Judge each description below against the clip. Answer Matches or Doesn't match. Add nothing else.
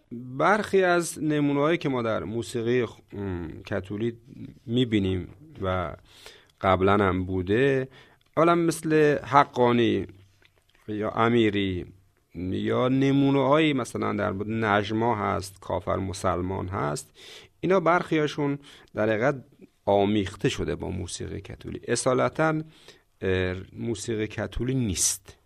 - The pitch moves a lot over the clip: Matches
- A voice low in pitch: Matches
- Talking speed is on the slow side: Matches